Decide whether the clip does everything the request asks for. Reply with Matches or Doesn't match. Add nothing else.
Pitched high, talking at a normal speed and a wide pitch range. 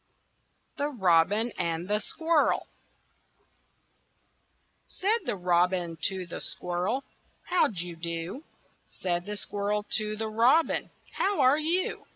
Doesn't match